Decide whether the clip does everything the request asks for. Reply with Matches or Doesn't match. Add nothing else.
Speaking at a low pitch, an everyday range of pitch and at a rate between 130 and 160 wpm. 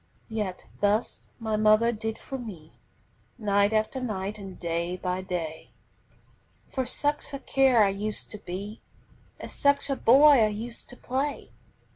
Doesn't match